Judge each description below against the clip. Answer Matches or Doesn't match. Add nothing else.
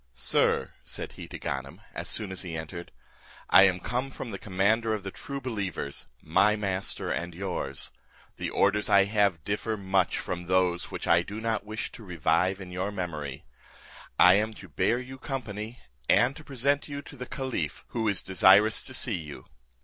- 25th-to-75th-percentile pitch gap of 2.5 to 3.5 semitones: Doesn't match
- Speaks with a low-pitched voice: Matches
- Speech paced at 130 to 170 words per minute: Doesn't match